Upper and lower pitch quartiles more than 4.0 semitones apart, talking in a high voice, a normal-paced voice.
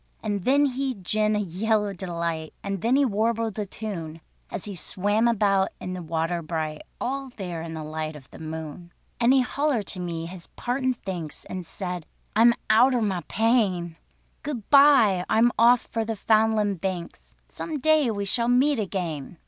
Yes: average, 5.3 semitones; high, 205 Hz; average, 180 wpm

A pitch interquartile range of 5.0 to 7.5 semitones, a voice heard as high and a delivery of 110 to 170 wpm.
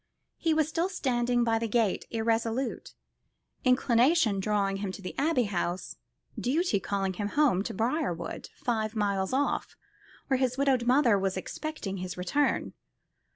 Yes: average, 5.3 semitones; high, 230 Hz; average, 145 wpm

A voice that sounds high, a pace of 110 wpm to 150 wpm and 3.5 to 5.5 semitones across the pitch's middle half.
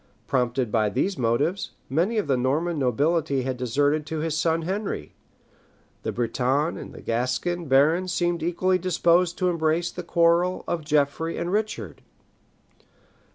No: medium, 160 Hz; average, 140 wpm; average, 4.6 semitones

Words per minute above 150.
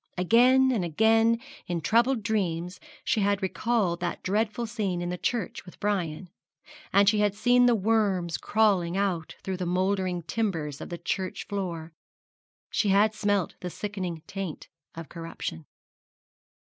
No: average, 145 wpm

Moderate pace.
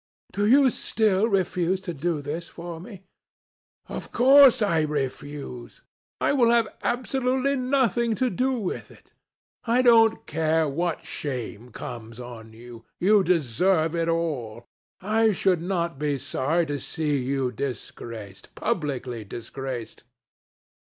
No: slow, 130 wpm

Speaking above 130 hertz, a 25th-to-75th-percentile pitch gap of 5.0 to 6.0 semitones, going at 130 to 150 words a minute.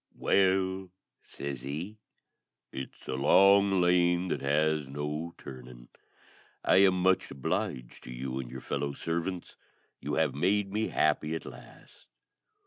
No: very low, 80 Hz; wide, 5.4 semitones; slow, 135 wpm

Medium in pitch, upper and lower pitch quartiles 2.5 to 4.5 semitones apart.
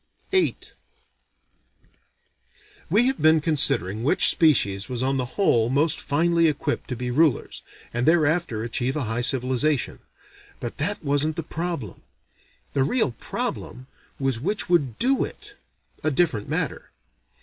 No: medium, 145 Hz; average, 5.0 semitones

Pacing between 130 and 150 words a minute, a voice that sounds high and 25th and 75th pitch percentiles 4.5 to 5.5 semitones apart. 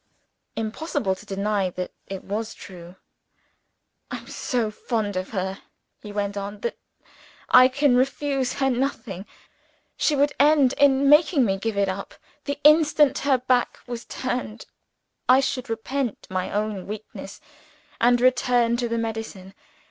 Yes: average, 145 wpm; high, 235 Hz; average, 4.9 semitones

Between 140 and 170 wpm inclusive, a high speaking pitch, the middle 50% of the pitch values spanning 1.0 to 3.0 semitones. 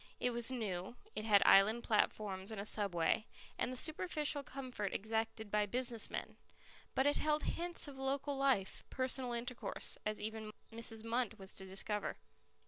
No: average, 160 wpm; high, 225 Hz; average, 4.0 semitones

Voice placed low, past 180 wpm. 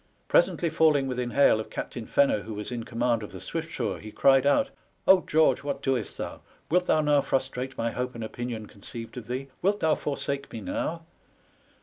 Yes: low, 130 Hz; average, 200 wpm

